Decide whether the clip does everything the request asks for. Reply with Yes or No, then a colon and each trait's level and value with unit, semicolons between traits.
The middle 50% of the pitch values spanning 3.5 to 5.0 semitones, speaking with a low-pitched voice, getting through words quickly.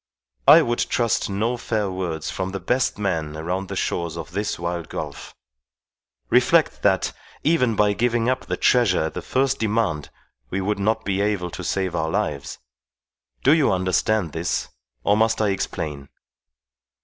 No: average, 4.6 semitones; low, 100 Hz; average, 160 wpm